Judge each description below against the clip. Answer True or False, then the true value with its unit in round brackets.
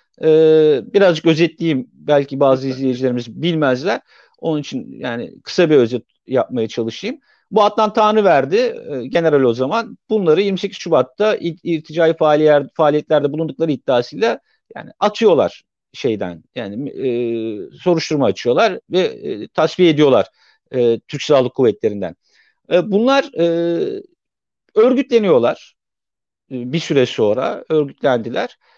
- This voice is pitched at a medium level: True (165 Hz)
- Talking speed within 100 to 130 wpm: True (115 wpm)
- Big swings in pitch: True (8.3 semitones)